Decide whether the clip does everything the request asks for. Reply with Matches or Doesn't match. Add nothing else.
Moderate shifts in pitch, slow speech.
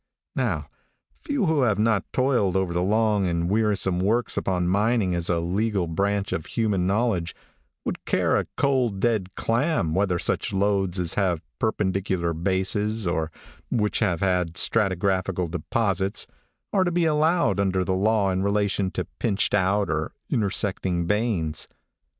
Doesn't match